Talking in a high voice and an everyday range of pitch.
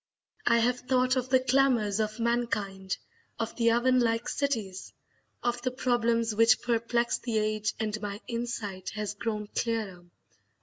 No: high, 230 Hz; narrow, 2.3 semitones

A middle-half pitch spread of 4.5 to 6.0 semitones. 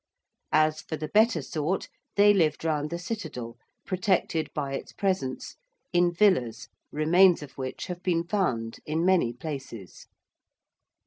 Yes: average, 5.1 semitones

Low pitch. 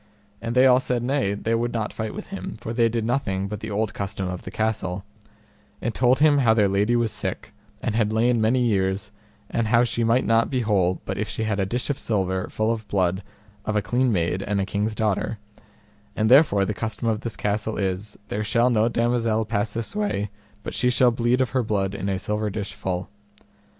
Yes: low, 110 Hz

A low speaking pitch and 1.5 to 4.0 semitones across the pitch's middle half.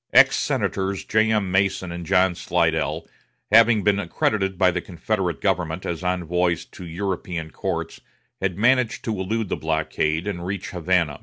Yes: very low, 95 Hz; average, 2.8 semitones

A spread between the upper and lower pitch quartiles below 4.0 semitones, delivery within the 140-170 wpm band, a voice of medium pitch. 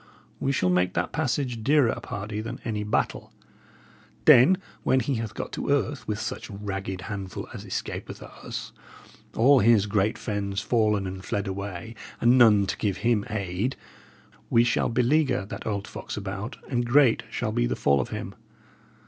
No: average, 3.6 semitones; average, 165 wpm; low, 110 Hz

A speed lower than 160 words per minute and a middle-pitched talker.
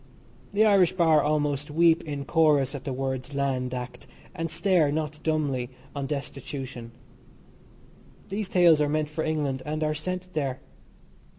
Yes: average, 150 wpm; medium, 150 Hz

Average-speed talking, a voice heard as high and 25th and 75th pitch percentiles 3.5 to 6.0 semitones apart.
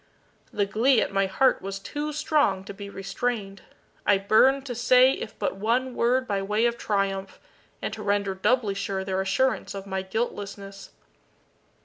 Yes: average, 165 wpm; high, 205 Hz; average, 3.8 semitones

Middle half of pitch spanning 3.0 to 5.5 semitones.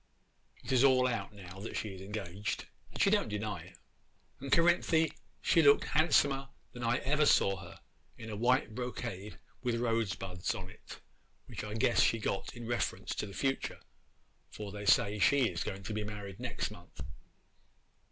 Yes: average, 4.5 semitones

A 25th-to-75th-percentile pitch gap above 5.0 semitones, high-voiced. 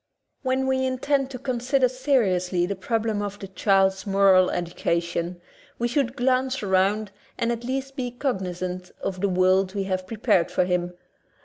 Yes: wide, 5.5 semitones; high, 205 Hz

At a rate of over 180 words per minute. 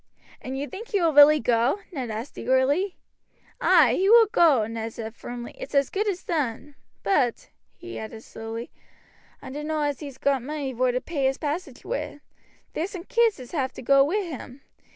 Yes: average, 190 wpm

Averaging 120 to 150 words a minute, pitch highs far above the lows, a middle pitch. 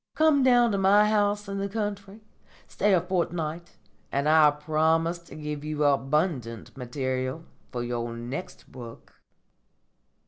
Yes: slow, 135 wpm; wide, 6.4 semitones; medium, 160 Hz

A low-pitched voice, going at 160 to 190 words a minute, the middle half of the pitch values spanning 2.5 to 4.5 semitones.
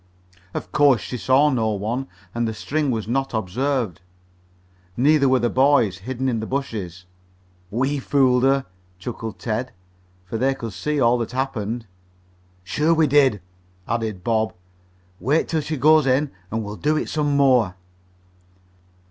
No: low, 125 Hz; average, 150 wpm; average, 4.0 semitones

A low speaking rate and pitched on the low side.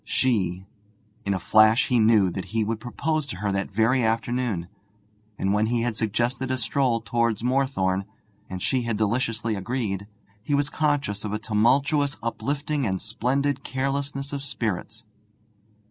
No: average, 155 wpm; low, 115 Hz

